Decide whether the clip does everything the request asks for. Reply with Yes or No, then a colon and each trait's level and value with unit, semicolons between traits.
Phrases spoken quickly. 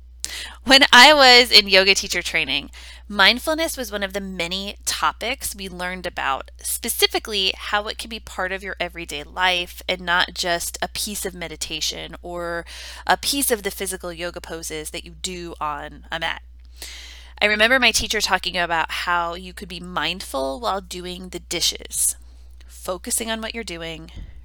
No: average, 165 wpm